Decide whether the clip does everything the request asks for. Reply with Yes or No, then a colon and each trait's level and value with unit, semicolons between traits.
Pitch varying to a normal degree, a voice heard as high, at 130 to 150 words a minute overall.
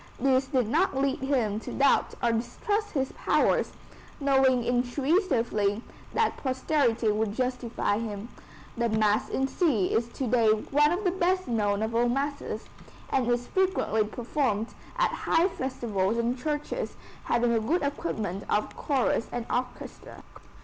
Yes: average, 4.0 semitones; high, 245 Hz; average, 145 wpm